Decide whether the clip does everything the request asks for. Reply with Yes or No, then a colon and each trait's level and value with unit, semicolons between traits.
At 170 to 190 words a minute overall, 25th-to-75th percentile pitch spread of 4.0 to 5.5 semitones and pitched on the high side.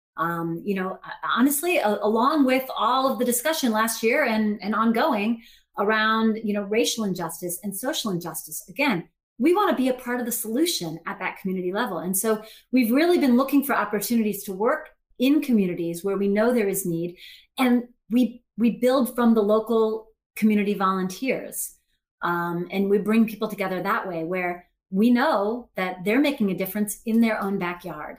Yes: average, 180 wpm; average, 4.3 semitones; high, 220 Hz